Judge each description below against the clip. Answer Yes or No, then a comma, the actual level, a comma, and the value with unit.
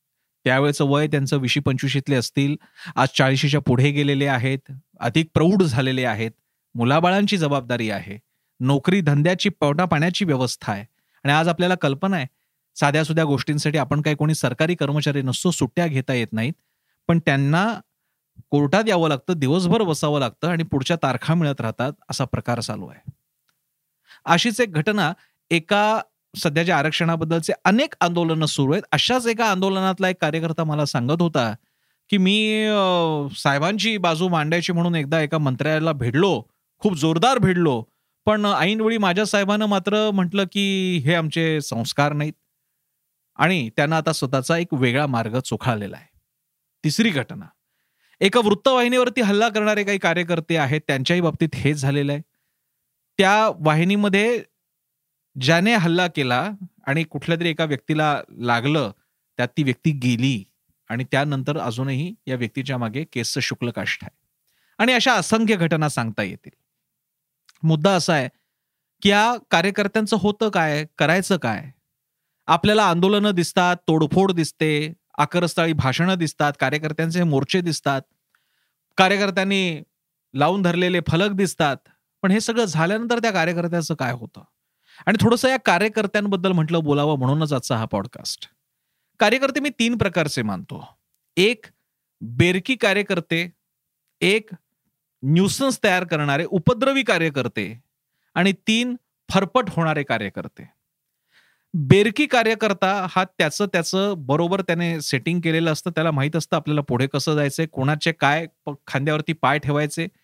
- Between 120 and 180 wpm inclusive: Yes, fast, 130 wpm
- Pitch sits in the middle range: Yes, medium, 160 Hz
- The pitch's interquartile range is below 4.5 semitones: No, average, 5.1 semitones